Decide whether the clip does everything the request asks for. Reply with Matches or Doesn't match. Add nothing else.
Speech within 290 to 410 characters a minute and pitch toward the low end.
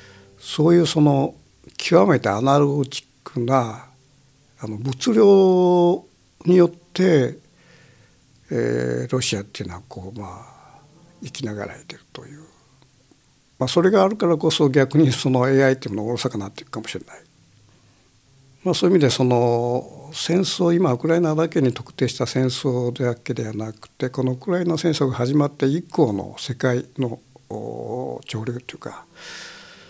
Matches